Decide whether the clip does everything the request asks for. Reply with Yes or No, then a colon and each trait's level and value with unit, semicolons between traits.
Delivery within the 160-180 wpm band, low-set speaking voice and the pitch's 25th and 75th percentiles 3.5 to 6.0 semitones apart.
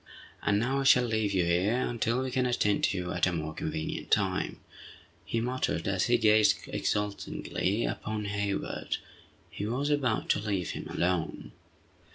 Yes: average, 165 wpm; low, 105 Hz; average, 4.1 semitones